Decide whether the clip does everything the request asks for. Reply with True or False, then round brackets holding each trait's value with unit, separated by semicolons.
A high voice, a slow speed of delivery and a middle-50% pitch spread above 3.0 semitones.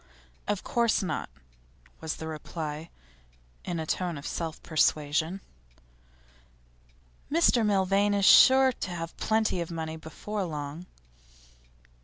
False (170 Hz; 115 wpm; 4.4 semitones)